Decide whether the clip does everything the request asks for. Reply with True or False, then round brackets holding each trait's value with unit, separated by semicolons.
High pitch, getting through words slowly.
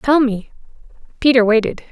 True (245 Hz; 125 wpm)